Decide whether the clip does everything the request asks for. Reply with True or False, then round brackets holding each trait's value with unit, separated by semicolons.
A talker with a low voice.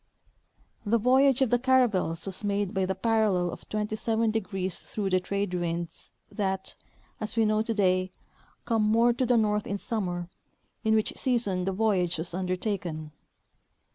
False (205 Hz)